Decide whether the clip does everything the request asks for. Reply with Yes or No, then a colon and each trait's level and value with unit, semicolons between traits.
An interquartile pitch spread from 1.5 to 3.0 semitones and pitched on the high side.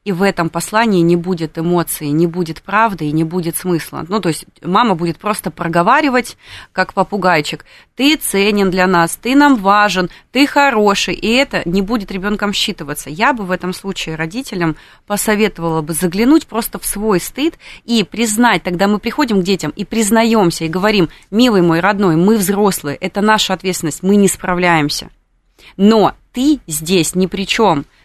No: average, 4.0 semitones; high, 195 Hz